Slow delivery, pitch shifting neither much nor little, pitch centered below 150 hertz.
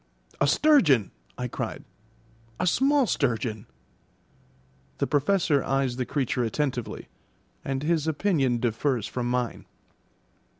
Yes: slow, 110 wpm; average, 4.5 semitones; low, 135 Hz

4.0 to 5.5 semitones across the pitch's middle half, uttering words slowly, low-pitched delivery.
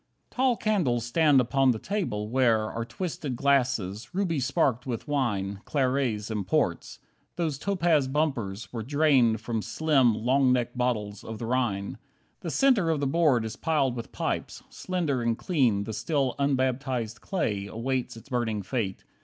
No: average, 4.7 semitones; average, 160 wpm; low, 130 Hz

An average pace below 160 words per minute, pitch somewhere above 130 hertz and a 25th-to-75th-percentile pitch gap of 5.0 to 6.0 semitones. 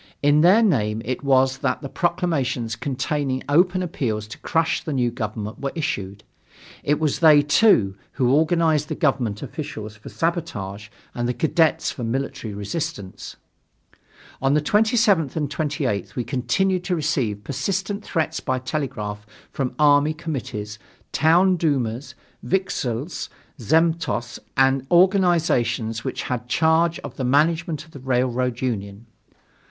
Yes: slow, 135 wpm; medium, 140 Hz; average, 5.3 semitones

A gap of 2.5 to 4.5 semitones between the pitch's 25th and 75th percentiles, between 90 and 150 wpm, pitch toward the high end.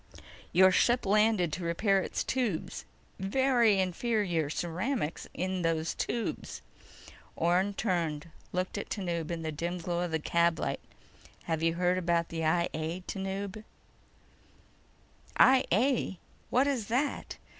No: average, 4.0 semitones; slow, 135 wpm; medium, 180 Hz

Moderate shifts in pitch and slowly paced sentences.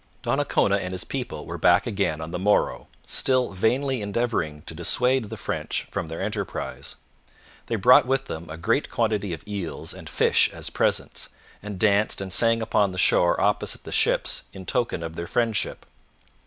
No: average, 4.7 semitones; average, 175 wpm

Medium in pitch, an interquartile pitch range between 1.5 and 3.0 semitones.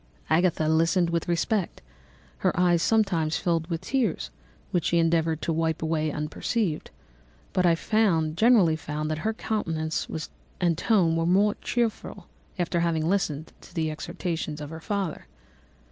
Yes: medium, 165 Hz; narrow, 2.5 semitones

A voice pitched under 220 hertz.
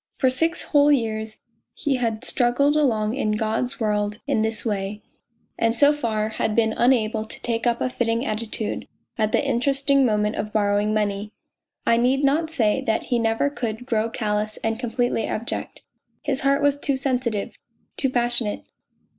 No: high, 230 Hz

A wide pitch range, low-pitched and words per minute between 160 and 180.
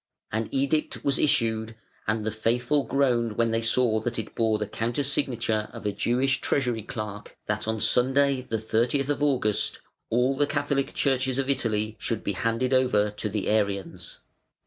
No: average, 3.5 semitones; low, 115 Hz; average, 170 wpm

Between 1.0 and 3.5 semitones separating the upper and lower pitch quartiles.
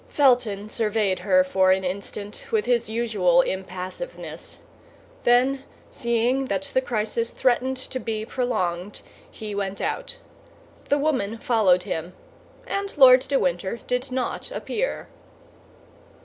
No: average, 4.9 semitones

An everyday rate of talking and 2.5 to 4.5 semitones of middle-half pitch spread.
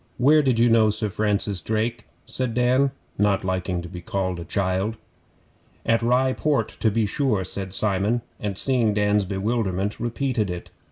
Yes: average, 160 wpm; average, 3.6 semitones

